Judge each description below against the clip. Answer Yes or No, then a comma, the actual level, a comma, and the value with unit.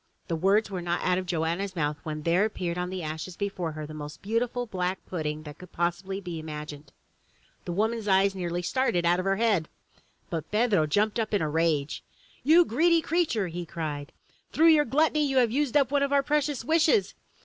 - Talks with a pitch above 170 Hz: Yes, medium, 185 Hz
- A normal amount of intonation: No, wide, 6.3 semitones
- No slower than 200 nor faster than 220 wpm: Yes, fast, 205 wpm